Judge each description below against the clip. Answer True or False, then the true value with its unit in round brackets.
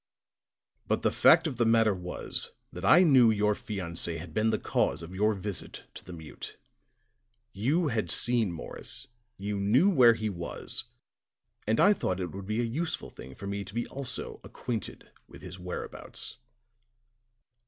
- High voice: False (105 Hz)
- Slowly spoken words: False (165 wpm)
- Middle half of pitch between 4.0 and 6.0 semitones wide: True (4.5 semitones)